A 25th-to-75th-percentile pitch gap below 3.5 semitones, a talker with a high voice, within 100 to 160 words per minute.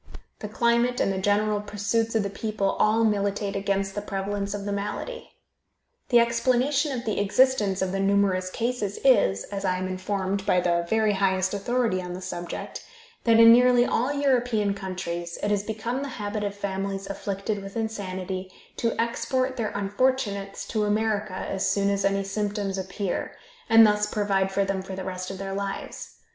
No: narrow, 2.5 semitones; high, 200 Hz; average, 180 wpm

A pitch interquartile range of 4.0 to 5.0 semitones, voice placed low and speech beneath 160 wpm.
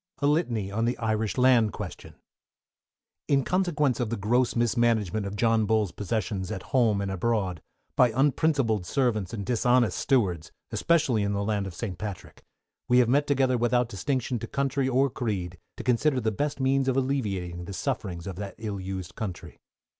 No: average, 4.5 semitones; low, 115 Hz; average, 175 wpm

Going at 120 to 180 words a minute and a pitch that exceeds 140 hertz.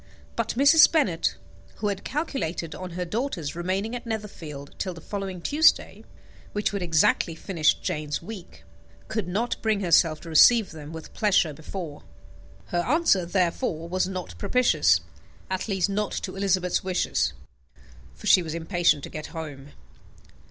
Yes: average, 150 wpm; medium, 185 Hz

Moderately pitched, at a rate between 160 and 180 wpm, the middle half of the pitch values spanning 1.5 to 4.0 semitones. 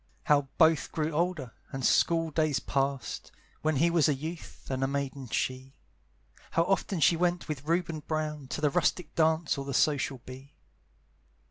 Yes: medium, 150 Hz; average, 165 wpm; average, 3.1 semitones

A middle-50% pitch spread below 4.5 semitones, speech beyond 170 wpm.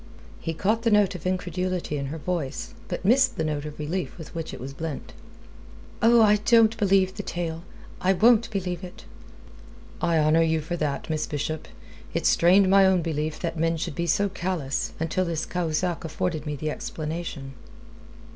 Yes: average, 3.4 semitones; average, 180 wpm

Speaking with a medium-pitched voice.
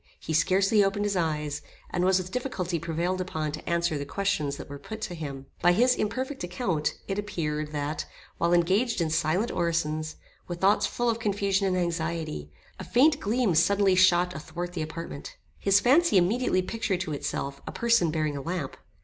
Yes: medium, 175 Hz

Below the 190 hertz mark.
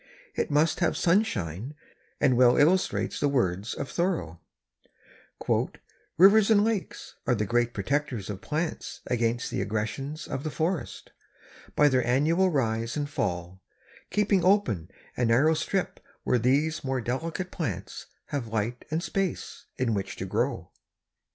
Yes: low, 135 Hz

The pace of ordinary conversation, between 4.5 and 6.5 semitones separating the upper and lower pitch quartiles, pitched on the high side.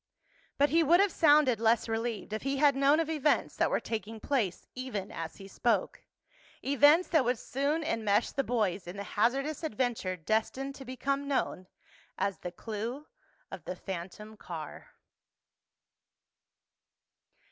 Yes: average, 145 wpm; wide, 5.5 semitones; high, 240 Hz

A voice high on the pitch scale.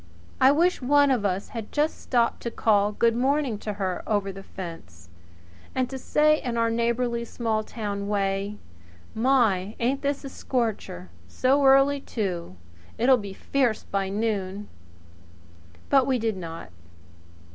Yes: high, 230 Hz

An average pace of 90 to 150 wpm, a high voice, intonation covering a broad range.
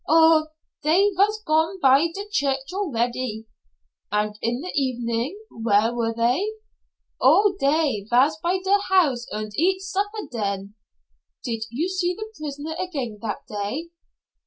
Yes: slow, 135 wpm; very high, 290 Hz; wide, 7.9 semitones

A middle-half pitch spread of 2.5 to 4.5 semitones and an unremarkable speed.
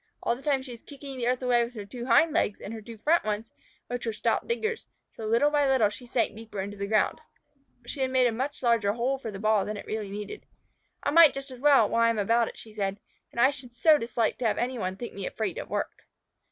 No: average, 3.7 semitones; fast, 265 wpm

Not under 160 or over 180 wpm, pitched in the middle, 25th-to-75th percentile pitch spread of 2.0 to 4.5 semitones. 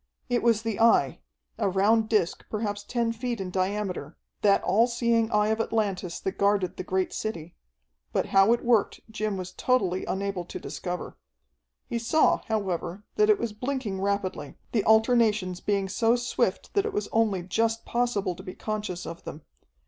No: average, 170 wpm; high, 210 Hz; average, 3.4 semitones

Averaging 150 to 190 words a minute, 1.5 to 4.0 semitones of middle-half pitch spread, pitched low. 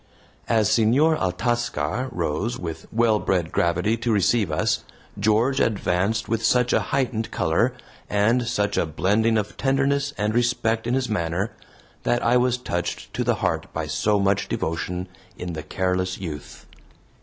No: average, 155 wpm; average, 4.7 semitones; low, 110 Hz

